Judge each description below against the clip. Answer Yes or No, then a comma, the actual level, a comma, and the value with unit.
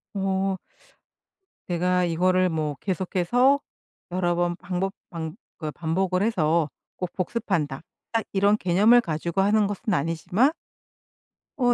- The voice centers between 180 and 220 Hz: Yes, medium, 185 Hz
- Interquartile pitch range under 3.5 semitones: Yes, average, 2.8 semitones